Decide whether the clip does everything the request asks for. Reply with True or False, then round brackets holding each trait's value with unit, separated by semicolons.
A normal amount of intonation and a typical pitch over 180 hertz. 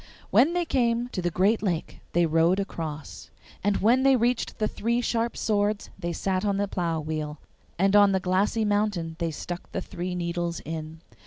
True (4.2 semitones; 190 Hz)